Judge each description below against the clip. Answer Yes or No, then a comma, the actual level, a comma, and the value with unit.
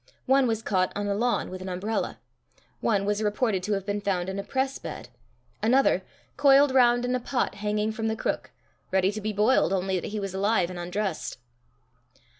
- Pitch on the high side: Yes, high, 210 Hz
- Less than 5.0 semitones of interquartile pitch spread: Yes, average, 3.9 semitones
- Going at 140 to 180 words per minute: No, average, 200 wpm